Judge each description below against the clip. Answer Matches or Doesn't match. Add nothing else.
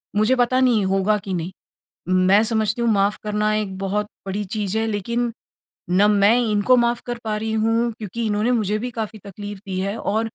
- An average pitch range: Doesn't match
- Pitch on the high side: Matches